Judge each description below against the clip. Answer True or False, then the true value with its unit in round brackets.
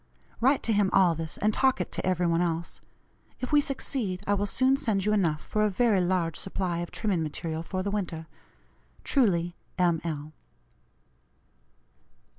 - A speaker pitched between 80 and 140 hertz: False (185 Hz)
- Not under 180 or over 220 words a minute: False (170 wpm)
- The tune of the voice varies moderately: True (4.0 semitones)